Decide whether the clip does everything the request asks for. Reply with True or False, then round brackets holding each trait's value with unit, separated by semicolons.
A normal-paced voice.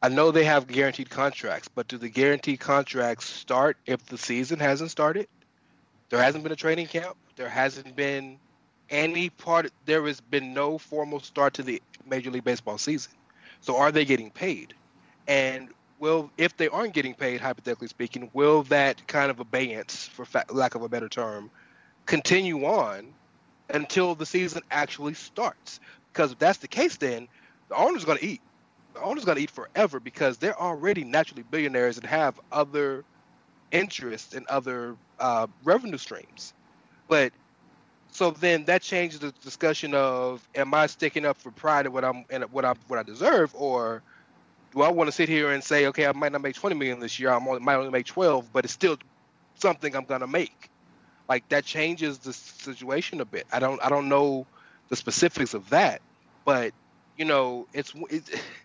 True (185 wpm)